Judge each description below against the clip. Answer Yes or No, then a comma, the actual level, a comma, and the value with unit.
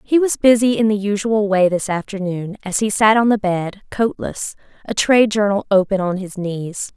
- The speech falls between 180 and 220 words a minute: Yes, average, 200 wpm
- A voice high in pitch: Yes, high, 205 Hz